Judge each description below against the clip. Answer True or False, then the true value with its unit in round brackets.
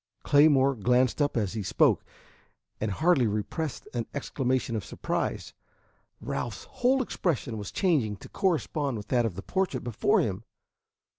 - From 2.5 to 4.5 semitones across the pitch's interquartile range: False (5.4 semitones)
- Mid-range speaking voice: False (125 Hz)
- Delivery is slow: False (145 wpm)